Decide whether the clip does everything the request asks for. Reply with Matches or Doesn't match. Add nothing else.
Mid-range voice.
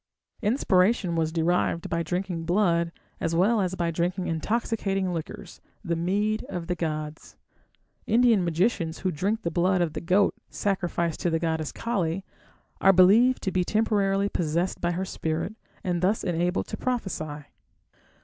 Matches